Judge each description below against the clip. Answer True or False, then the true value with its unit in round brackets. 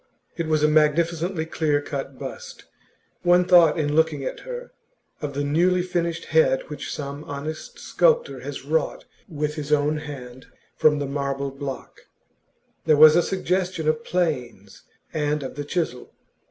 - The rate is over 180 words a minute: False (155 wpm)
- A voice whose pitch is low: False (155 Hz)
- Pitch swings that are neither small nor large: True (3.3 semitones)